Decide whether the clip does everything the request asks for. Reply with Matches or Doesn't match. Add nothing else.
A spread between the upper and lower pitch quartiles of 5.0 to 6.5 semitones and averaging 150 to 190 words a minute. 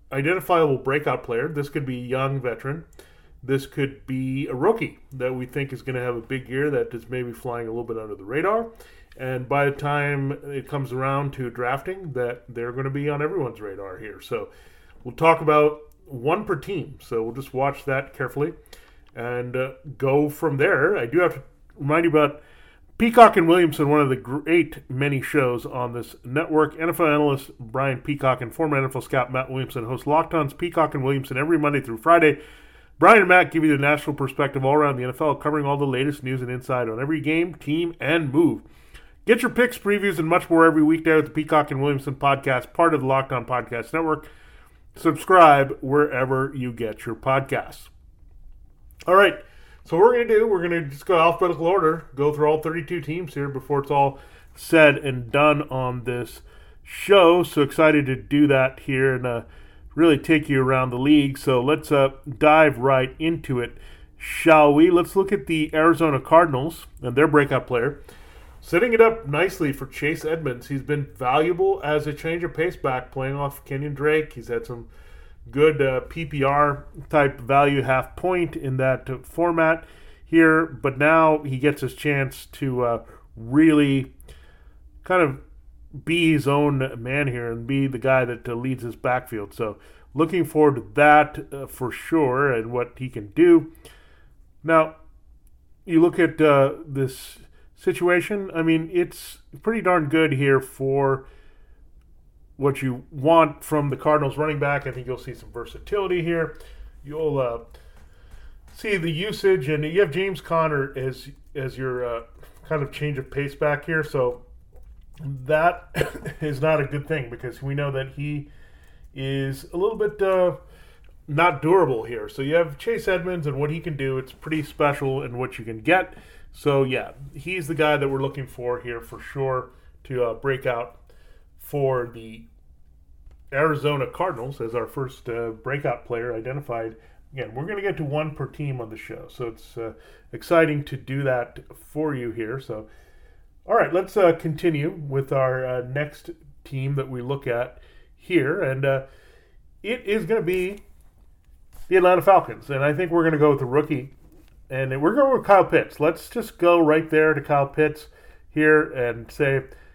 Doesn't match